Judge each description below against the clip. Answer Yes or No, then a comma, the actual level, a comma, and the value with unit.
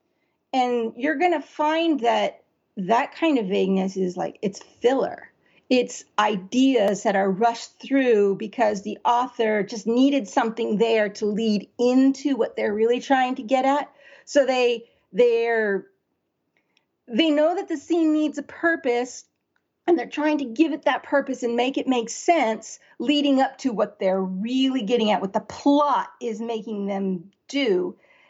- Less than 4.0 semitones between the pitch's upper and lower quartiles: No, average, 4.6 semitones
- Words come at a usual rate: Yes, average, 160 wpm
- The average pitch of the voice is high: Yes, high, 245 Hz